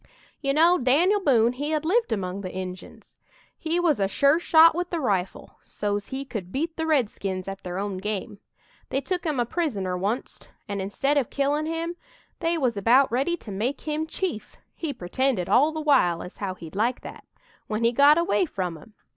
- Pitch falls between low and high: No, very high, 260 Hz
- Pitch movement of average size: No, wide, 7.9 semitones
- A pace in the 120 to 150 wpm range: No, average, 195 wpm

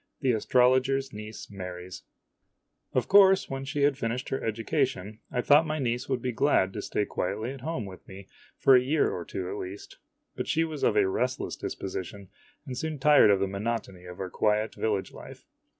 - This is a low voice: Yes, low, 120 Hz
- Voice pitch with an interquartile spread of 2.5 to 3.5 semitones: No, wide, 5.5 semitones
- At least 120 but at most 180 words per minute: No, average, 195 wpm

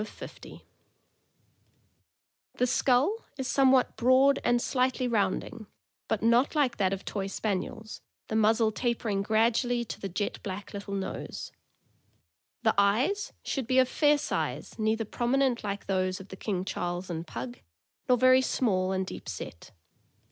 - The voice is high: Yes, high, 220 Hz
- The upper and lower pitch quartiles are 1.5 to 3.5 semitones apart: No, average, 4.4 semitones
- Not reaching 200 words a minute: Yes, average, 150 wpm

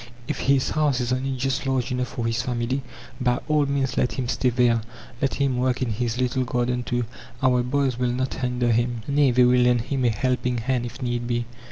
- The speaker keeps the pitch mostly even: Yes, narrow, 1.3 semitones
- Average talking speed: No, fast, 220 wpm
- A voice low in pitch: Yes, low, 125 Hz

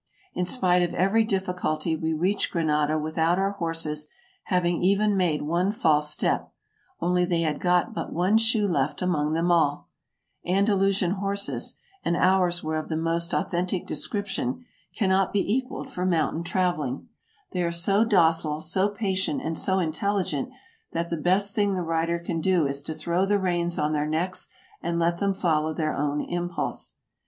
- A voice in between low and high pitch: Yes, medium, 175 Hz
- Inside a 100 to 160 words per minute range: No, average, 175 wpm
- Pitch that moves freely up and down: No, average, 3.1 semitones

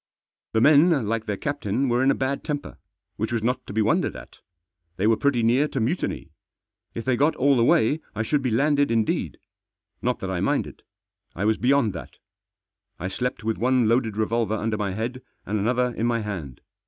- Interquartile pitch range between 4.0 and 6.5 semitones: No, average, 3.4 semitones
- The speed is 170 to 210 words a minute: Yes, average, 200 wpm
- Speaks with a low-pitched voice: Yes, low, 115 Hz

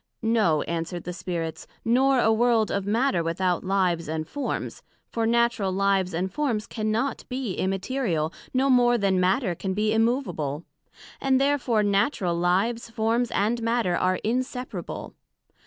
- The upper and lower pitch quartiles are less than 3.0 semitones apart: No, average, 4.9 semitones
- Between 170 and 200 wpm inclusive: No, average, 140 wpm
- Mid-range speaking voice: No, high, 215 Hz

